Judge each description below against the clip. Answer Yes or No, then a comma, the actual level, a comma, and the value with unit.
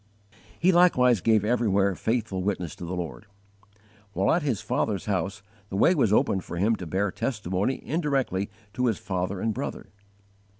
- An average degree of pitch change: Yes, average, 4.7 semitones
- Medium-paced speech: Yes, average, 165 wpm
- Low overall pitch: Yes, low, 100 Hz